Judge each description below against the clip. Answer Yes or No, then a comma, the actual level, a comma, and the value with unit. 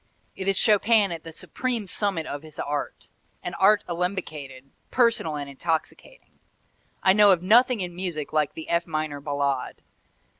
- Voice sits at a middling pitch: Yes, medium, 170 Hz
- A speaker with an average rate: Yes, average, 155 wpm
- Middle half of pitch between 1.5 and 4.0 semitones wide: No, average, 4.9 semitones